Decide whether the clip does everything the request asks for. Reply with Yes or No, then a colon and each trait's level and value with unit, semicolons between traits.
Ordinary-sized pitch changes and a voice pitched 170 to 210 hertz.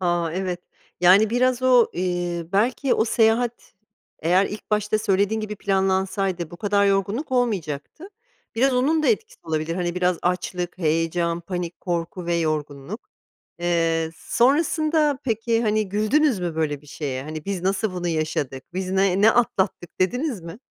Yes: average, 4.6 semitones; high, 190 Hz